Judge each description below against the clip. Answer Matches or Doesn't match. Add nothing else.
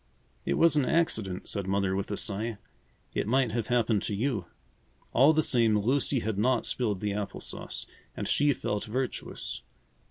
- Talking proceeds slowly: Doesn't match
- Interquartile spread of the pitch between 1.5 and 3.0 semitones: Doesn't match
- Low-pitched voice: Matches